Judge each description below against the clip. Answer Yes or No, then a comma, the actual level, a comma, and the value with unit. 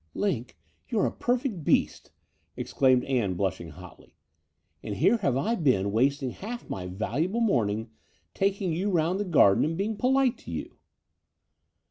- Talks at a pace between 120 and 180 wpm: Yes, average, 145 wpm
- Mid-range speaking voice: Yes, medium, 155 Hz